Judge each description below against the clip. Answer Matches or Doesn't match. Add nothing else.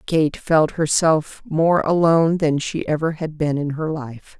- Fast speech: Doesn't match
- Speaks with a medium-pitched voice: Matches